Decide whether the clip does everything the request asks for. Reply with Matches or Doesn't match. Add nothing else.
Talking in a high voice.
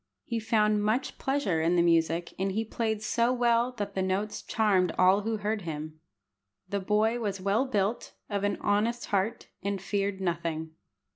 Matches